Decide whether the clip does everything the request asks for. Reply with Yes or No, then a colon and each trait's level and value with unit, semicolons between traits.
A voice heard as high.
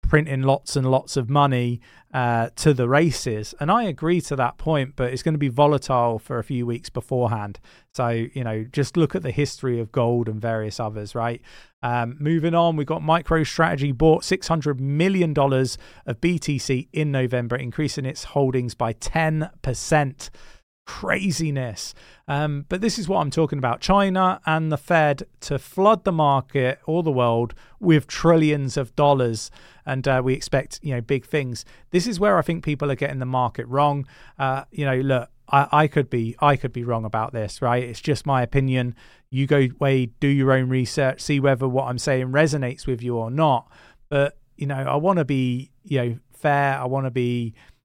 No: low, 135 Hz